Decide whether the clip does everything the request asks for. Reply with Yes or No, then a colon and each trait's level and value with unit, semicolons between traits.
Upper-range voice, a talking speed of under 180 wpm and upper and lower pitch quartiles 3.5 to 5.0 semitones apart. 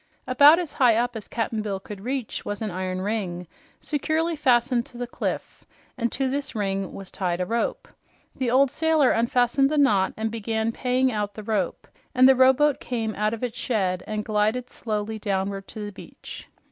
No: high, 225 Hz; average, 190 wpm; average, 3.9 semitones